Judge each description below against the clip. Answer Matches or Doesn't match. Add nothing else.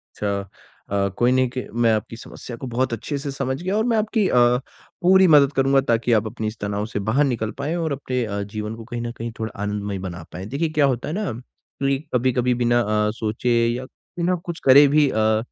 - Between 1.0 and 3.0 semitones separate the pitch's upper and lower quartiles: Doesn't match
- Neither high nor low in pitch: Doesn't match